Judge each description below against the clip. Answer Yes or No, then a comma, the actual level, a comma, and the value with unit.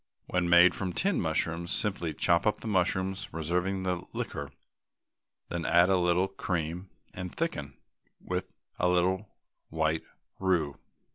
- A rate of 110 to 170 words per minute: Yes, slow, 135 wpm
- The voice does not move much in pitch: Yes, narrow, 2.2 semitones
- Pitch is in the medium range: No, very low, 90 Hz